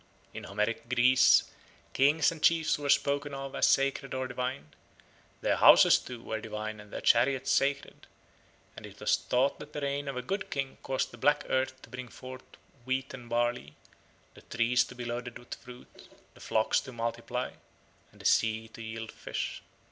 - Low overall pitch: Yes, low, 125 Hz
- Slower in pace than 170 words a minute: No, average, 180 wpm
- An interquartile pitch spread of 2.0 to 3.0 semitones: Yes, average, 2.7 semitones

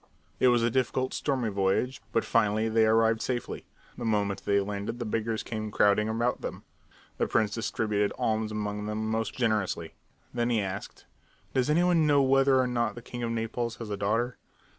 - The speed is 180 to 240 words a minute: Yes, average, 185 wpm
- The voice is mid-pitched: No, low, 115 Hz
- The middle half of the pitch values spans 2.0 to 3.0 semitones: Yes, narrow, 2.5 semitones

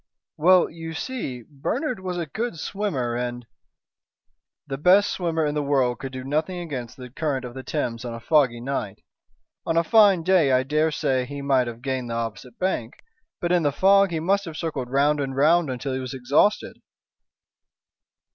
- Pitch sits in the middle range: Yes, medium, 145 Hz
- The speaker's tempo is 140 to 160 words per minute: No, average, 190 wpm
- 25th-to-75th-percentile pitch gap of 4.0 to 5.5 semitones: Yes, average, 5.1 semitones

